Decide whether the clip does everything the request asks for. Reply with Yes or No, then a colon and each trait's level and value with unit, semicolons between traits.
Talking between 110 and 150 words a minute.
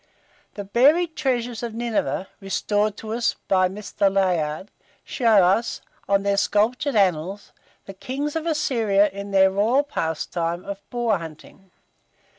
Yes: slow, 135 wpm